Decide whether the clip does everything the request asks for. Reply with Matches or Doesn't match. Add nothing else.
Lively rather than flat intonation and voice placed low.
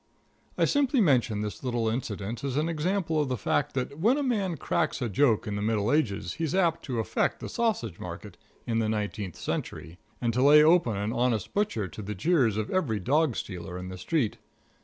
Matches